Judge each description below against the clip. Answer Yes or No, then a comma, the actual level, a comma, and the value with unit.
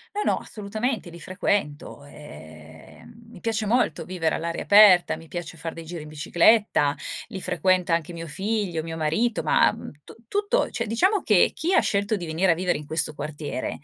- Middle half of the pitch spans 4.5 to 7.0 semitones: Yes, average, 5.2 semitones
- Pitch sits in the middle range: Yes, medium, 175 Hz